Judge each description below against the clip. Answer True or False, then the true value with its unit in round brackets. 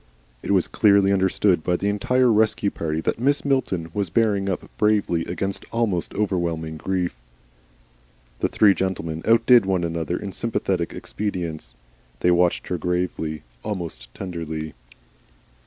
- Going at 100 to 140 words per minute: True (135 wpm)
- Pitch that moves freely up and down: False (3.6 semitones)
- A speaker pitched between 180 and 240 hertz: False (95 Hz)